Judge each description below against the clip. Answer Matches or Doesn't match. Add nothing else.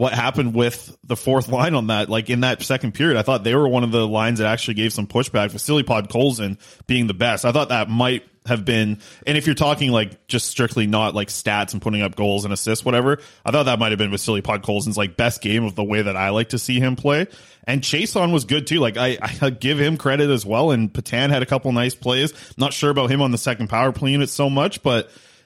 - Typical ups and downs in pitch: Matches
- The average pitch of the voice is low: Matches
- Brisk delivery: Matches